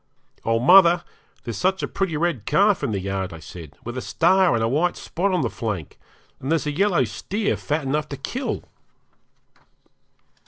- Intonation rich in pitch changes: Yes, wide, 8.1 semitones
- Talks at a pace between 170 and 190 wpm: Yes, average, 185 wpm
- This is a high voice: No, medium, 150 Hz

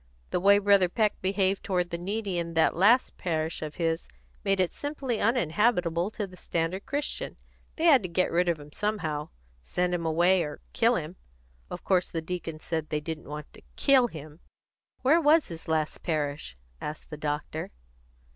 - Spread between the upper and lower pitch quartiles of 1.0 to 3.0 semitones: No, average, 4.2 semitones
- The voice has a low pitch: No, medium, 175 Hz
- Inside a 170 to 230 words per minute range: Yes, average, 180 wpm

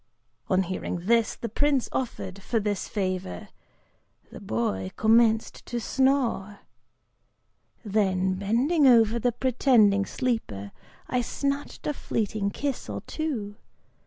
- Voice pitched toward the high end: Yes, high, 220 Hz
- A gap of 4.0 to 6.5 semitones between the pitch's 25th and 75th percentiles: Yes, average, 4.5 semitones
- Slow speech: Yes, slow, 110 wpm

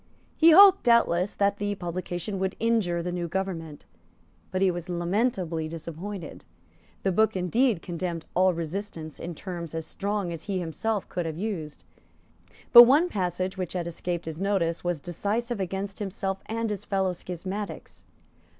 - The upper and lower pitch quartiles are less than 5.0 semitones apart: Yes, average, 3.1 semitones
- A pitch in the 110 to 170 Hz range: No, medium, 185 Hz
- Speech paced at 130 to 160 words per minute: Yes, average, 155 wpm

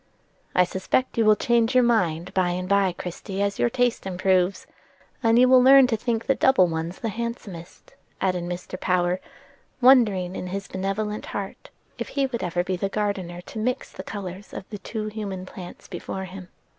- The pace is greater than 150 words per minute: Yes, average, 185 wpm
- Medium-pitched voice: No, high, 195 Hz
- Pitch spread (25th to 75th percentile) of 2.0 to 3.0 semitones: No, average, 4.0 semitones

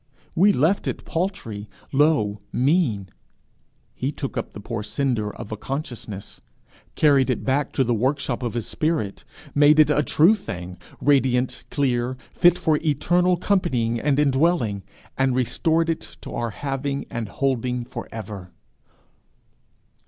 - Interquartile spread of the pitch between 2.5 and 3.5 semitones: No, average, 4.7 semitones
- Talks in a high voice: No, low, 130 Hz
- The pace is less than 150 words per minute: Yes, average, 140 wpm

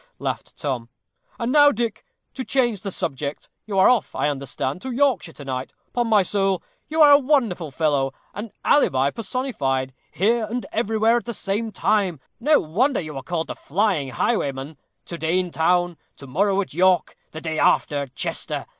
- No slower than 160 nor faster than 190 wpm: Yes, average, 180 wpm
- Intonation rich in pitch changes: Yes, wide, 7.8 semitones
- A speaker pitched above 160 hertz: Yes, high, 190 Hz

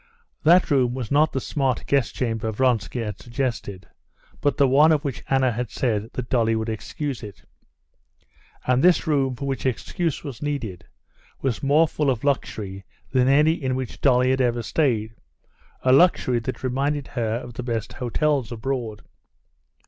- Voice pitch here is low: Yes, low, 130 Hz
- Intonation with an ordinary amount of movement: Yes, average, 3.4 semitones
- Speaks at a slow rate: No, average, 165 wpm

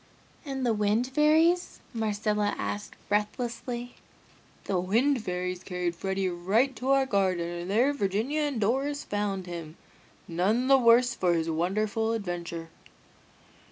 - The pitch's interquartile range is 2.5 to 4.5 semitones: No, wide, 5.5 semitones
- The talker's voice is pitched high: Yes, high, 210 Hz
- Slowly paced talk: Yes, slow, 130 wpm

